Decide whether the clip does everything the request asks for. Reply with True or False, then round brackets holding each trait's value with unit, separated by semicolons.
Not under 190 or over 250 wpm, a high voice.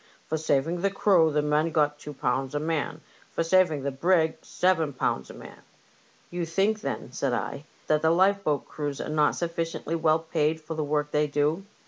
False (195 wpm; 155 Hz)